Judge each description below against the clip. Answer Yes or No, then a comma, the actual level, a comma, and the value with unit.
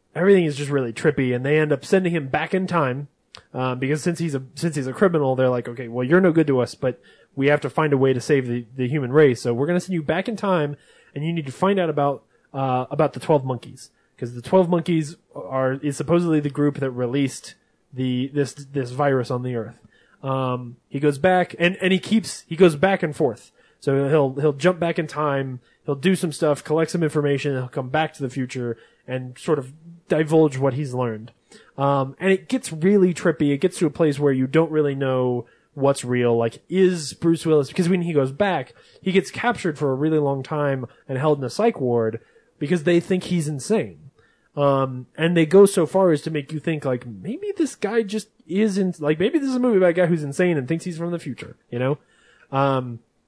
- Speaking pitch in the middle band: Yes, medium, 150 Hz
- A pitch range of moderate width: Yes, average, 4.5 semitones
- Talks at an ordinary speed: No, fast, 235 wpm